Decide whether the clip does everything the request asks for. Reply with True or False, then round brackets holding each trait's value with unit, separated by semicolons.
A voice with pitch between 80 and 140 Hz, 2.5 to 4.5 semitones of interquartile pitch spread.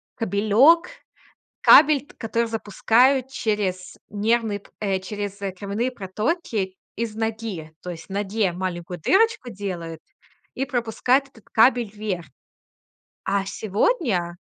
False (215 Hz; 4.1 semitones)